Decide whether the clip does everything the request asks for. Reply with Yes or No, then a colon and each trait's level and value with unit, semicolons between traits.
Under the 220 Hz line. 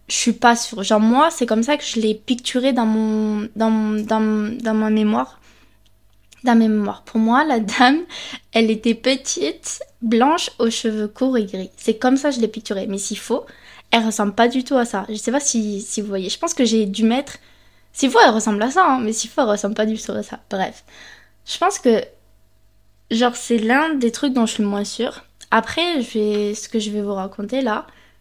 No: high, 225 Hz